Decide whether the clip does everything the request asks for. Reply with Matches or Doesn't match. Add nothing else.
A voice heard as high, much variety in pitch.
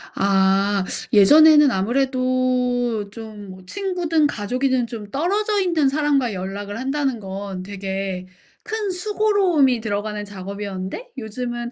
Matches